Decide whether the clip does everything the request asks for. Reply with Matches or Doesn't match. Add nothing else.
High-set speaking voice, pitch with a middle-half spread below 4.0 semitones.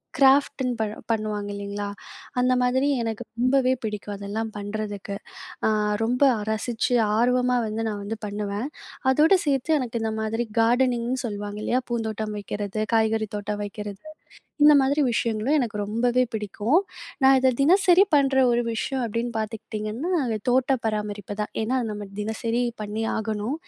Matches